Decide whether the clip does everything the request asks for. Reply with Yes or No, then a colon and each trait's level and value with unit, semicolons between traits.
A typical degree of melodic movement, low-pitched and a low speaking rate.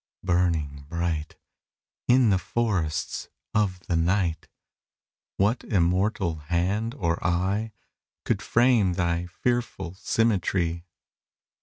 Yes: average, 3.8 semitones; very low, 90 Hz; slow, 95 wpm